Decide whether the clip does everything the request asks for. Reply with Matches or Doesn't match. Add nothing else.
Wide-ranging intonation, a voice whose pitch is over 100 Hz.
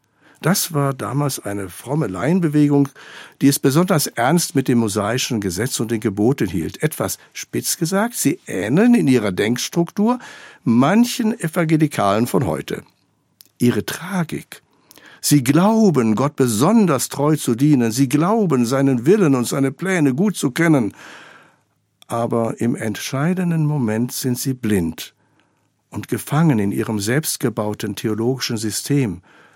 Matches